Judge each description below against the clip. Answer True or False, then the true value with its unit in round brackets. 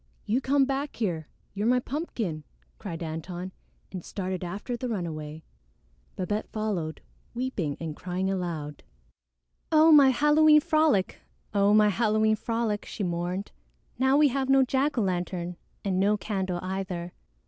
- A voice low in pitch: False (200 Hz)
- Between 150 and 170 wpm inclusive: False (140 wpm)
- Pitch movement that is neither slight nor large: False (6.2 semitones)